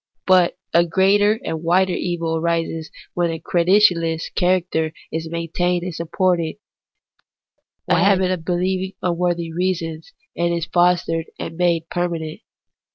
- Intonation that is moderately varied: No, narrow, 1.7 semitones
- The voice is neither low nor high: Yes, medium, 170 Hz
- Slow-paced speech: Yes, slow, 130 wpm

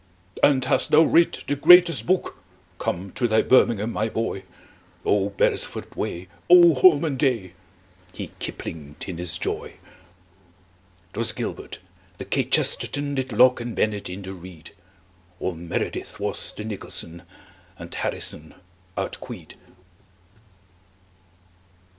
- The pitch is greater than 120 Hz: No, low, 110 Hz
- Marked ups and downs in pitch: Yes, wide, 7.3 semitones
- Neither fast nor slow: No, slow, 115 wpm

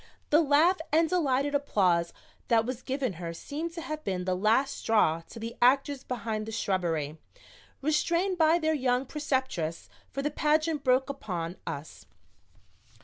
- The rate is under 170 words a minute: Yes, average, 150 wpm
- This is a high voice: Yes, very high, 260 Hz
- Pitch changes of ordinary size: No, wide, 7.4 semitones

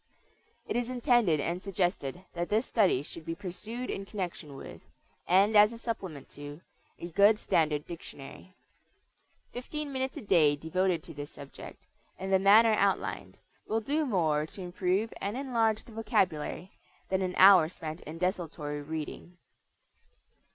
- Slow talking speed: No, average, 150 wpm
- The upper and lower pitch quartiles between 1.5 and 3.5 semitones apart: No, average, 5.3 semitones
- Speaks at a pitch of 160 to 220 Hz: Yes, medium, 185 Hz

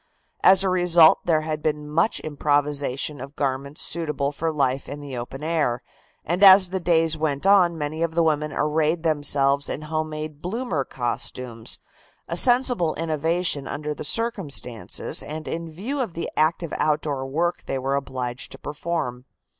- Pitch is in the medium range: Yes, medium, 155 Hz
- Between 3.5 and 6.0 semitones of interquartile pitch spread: No, average, 3.1 semitones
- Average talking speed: Yes, average, 160 wpm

